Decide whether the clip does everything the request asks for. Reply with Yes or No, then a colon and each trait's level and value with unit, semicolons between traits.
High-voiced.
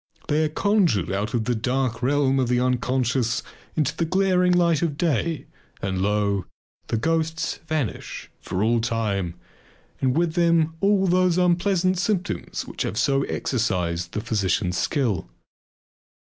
No: low, 135 Hz